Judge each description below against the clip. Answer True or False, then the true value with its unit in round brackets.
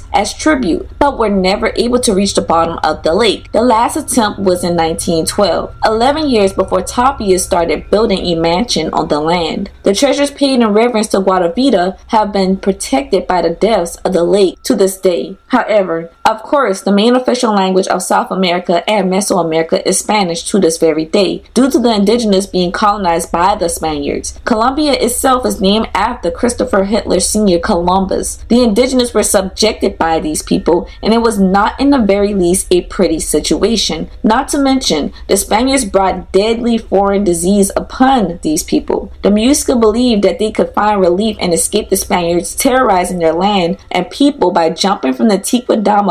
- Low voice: False (200 Hz)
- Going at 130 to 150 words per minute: False (180 wpm)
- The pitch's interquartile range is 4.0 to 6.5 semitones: True (4.5 semitones)